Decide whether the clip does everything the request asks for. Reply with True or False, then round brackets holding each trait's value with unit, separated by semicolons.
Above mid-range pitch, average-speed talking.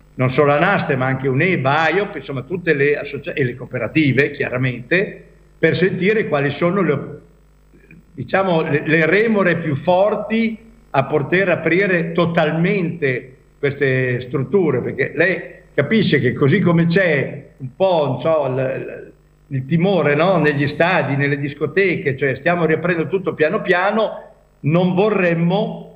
False (160 Hz; 140 wpm)